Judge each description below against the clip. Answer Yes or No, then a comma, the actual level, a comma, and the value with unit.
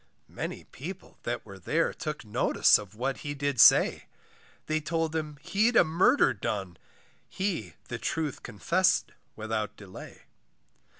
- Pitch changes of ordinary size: No, wide, 7.4 semitones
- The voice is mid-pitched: Yes, medium, 145 Hz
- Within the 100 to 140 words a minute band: Yes, slow, 135 wpm